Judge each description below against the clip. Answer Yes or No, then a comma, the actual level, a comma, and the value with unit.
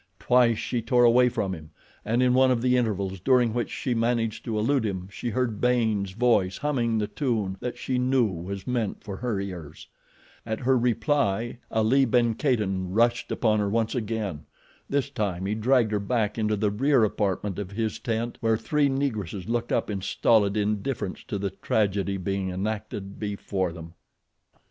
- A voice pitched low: Yes, low, 110 Hz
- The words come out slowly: No, average, 175 wpm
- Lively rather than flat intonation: No, average, 3.6 semitones